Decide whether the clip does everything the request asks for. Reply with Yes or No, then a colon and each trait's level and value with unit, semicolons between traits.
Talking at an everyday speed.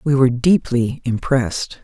No: slow, 130 wpm